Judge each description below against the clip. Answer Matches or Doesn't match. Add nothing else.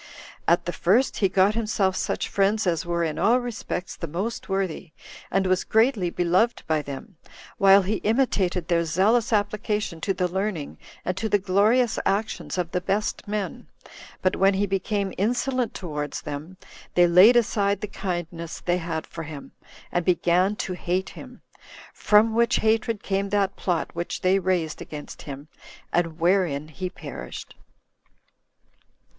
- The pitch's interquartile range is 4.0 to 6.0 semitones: Doesn't match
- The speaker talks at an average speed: Matches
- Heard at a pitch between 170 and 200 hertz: Matches